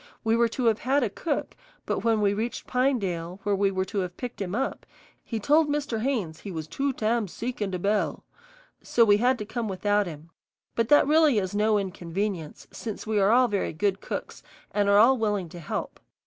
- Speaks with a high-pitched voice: Yes, high, 210 Hz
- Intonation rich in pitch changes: No, average, 3.8 semitones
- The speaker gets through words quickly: Yes, fast, 215 wpm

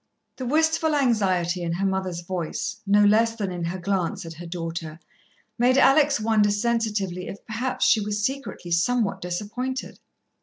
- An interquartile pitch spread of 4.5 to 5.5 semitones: Yes, average, 5.0 semitones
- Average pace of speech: Yes, average, 155 wpm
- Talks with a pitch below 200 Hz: No, high, 205 Hz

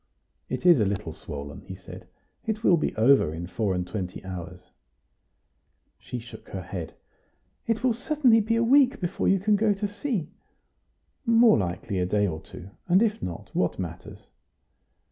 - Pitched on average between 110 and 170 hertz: Yes, low, 135 Hz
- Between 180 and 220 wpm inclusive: No, average, 170 wpm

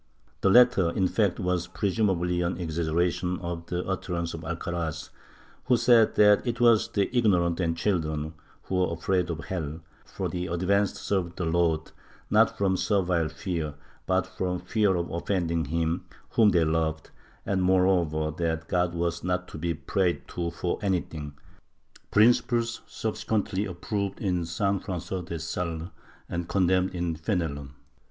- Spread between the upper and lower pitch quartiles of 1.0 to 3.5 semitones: Yes, narrow, 2.6 semitones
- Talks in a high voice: No, very low, 90 Hz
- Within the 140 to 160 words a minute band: Yes, average, 155 wpm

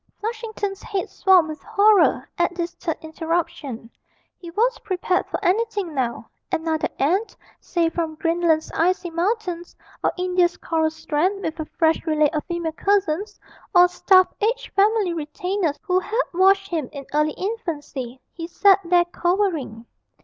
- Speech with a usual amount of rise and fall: Yes, average, 3.6 semitones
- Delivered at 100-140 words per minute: No, average, 150 wpm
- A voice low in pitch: No, very high, 350 Hz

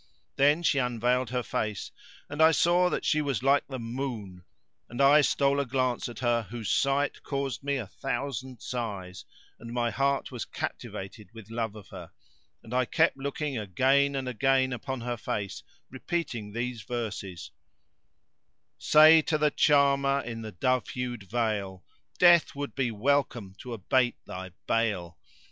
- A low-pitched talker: Yes, low, 125 Hz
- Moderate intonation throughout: Yes, average, 3.9 semitones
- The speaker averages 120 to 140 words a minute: No, average, 160 wpm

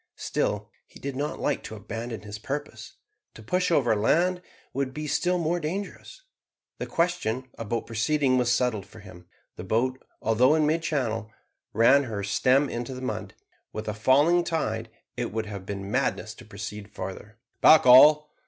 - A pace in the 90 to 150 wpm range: No, average, 170 wpm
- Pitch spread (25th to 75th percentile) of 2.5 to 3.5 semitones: No, wide, 5.6 semitones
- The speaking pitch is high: No, low, 125 Hz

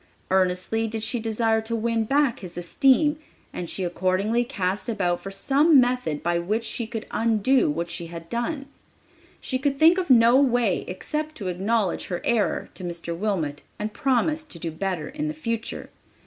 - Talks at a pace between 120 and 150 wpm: No, average, 175 wpm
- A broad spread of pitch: Yes, wide, 5.9 semitones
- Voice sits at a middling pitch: No, high, 225 Hz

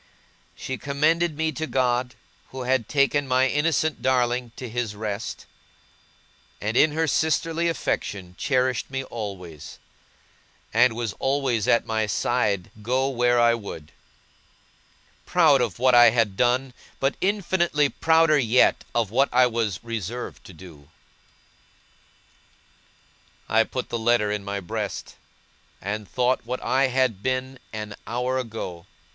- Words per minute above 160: No, slow, 135 wpm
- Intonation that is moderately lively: Yes, average, 3.5 semitones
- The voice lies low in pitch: Yes, low, 125 Hz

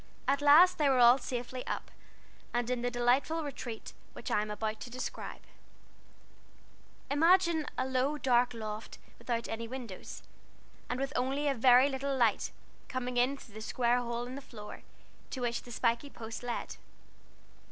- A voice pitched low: No, high, 245 Hz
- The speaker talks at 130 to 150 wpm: No, average, 165 wpm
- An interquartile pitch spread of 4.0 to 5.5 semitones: No, narrow, 2.6 semitones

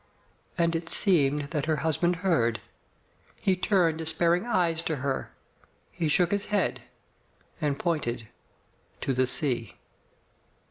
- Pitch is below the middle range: No, medium, 160 Hz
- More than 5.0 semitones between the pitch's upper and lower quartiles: No, average, 3.9 semitones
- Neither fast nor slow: No, slow, 125 wpm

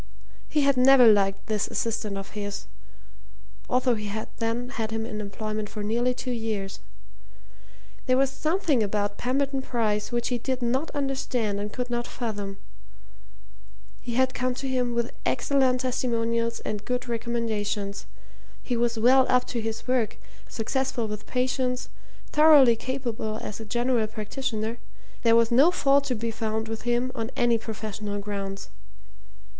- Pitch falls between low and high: No, high, 235 Hz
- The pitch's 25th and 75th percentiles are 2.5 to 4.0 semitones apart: Yes, average, 2.9 semitones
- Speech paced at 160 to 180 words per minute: No, average, 150 wpm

